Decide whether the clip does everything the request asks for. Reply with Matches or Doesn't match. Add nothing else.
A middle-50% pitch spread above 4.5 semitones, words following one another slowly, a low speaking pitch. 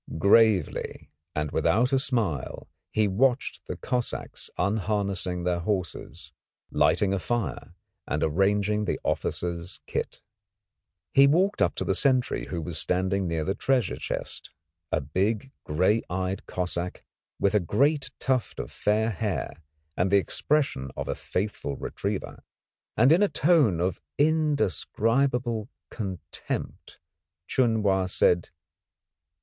Matches